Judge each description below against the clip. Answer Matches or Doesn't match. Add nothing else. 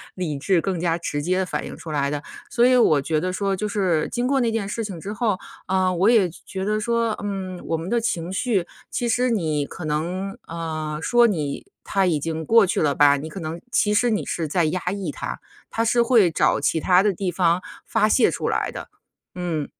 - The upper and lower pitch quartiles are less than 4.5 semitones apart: Doesn't match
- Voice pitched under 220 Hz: Matches